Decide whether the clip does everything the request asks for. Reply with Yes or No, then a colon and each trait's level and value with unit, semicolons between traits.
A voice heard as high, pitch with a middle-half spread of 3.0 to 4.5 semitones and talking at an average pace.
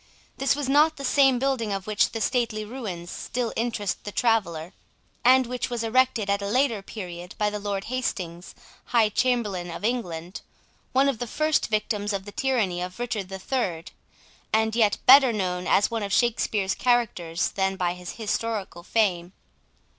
Yes: high, 215 Hz; average, 4.2 semitones; average, 170 wpm